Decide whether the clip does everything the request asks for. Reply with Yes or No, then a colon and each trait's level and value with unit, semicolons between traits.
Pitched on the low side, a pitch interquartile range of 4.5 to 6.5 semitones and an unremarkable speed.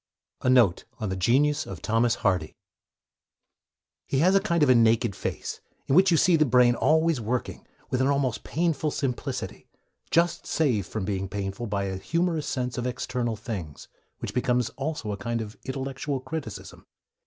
Yes: low, 125 Hz; wide, 5.4 semitones; average, 165 wpm